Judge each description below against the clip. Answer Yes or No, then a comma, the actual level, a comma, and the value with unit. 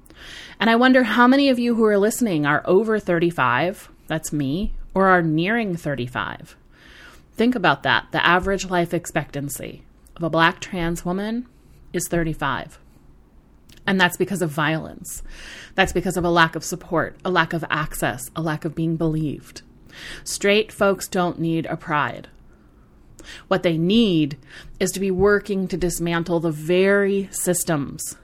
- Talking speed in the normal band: Yes, average, 155 wpm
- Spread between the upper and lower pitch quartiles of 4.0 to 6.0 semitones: No, average, 3.5 semitones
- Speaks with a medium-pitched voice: Yes, medium, 170 Hz